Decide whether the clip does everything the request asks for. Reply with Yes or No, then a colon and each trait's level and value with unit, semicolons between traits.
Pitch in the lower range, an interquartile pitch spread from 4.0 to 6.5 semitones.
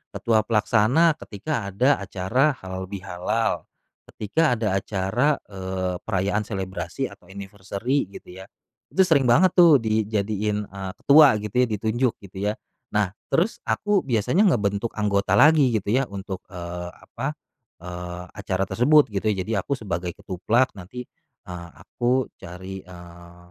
Yes: low, 105 Hz; average, 4.8 semitones